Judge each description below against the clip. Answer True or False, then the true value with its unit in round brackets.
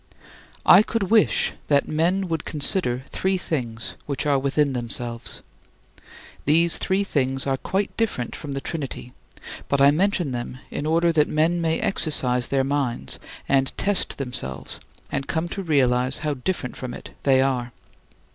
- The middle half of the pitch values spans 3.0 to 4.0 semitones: False (4.5 semitones)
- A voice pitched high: False (140 Hz)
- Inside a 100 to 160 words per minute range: True (155 wpm)